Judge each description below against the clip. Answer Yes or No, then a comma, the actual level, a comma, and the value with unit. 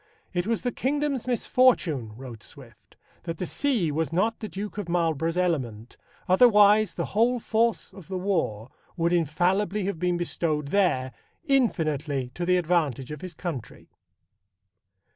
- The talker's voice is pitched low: No, medium, 175 Hz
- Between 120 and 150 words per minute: Yes, average, 145 wpm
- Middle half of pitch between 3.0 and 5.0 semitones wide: No, wide, 5.5 semitones